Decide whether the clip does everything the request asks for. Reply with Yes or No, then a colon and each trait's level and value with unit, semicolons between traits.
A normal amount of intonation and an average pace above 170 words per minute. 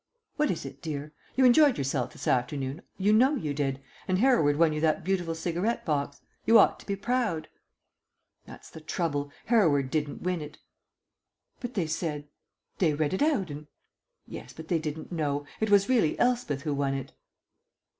No: wide, 5.9 semitones; average, 180 wpm